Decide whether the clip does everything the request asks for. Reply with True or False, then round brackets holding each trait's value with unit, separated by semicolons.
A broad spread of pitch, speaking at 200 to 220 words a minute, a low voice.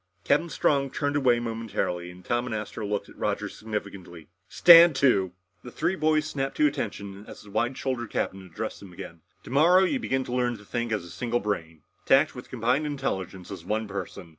True (5.7 semitones; 205 wpm; 120 Hz)